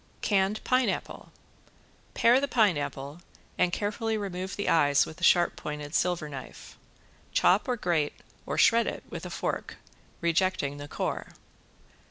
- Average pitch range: No, wide, 5.8 semitones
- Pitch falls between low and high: Yes, medium, 180 Hz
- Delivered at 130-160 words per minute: Yes, average, 140 wpm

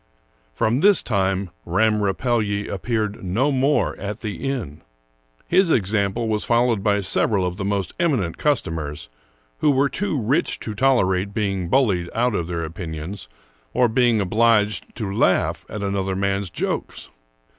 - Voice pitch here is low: Yes, low, 105 Hz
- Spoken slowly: No, average, 145 wpm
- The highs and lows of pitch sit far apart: No, average, 4.1 semitones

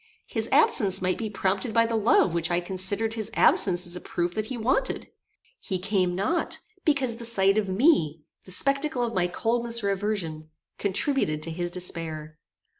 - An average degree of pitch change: Yes, average, 4.5 semitones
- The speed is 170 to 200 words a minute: Yes, average, 180 wpm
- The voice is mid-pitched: No, high, 195 Hz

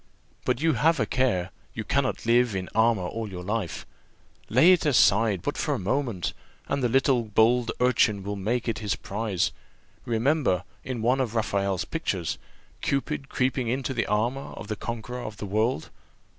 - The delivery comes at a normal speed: Yes, average, 170 wpm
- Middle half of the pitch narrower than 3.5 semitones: No, average, 4.0 semitones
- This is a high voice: No, low, 115 Hz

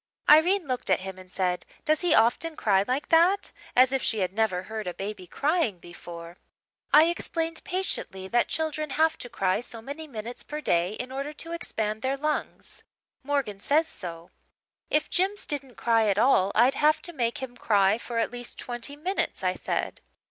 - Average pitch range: No, wide, 7.0 semitones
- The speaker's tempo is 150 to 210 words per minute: Yes, average, 185 wpm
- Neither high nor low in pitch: No, high, 245 Hz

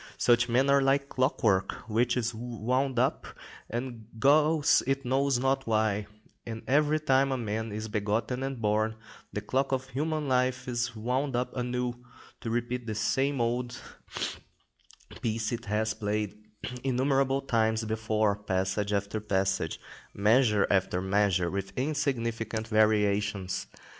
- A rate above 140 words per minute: No, slow, 135 wpm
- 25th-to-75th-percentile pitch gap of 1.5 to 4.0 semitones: Yes, average, 3.6 semitones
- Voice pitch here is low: Yes, low, 120 Hz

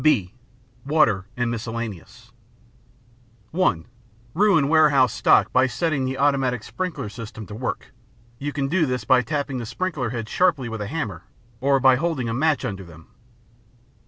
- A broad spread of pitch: No, average, 4.6 semitones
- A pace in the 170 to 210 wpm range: No, average, 155 wpm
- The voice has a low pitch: Yes, low, 130 Hz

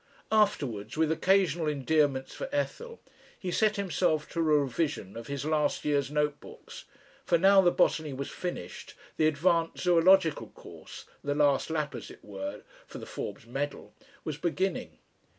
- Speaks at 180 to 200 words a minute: No, average, 155 wpm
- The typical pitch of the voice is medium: Yes, medium, 155 Hz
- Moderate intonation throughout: Yes, average, 4.0 semitones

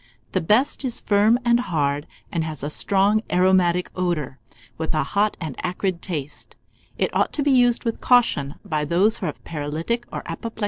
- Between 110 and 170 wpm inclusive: No, average, 190 wpm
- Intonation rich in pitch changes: Yes, wide, 6.1 semitones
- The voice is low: No, medium, 180 Hz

